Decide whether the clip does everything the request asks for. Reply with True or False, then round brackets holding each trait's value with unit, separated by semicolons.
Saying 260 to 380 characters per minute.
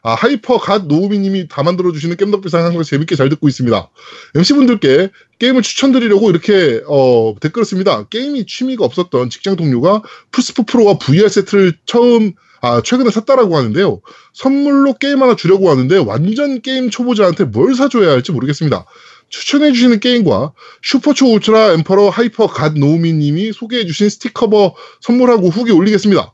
False (405 characters per minute)